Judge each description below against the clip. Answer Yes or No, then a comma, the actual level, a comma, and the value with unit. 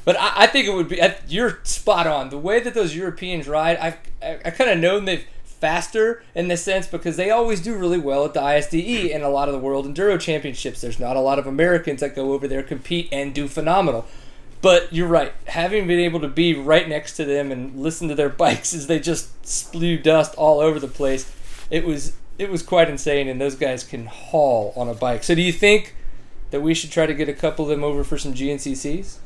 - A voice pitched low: No, medium, 155 Hz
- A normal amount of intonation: Yes, average, 3.5 semitones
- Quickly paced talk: Yes, fast, 240 wpm